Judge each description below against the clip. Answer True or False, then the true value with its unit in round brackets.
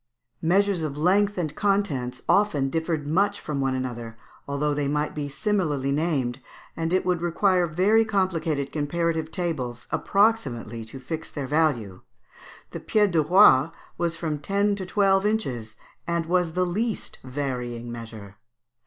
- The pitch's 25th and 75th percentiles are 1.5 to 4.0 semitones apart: False (5.5 semitones)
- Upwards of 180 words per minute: False (145 wpm)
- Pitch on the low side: False (160 Hz)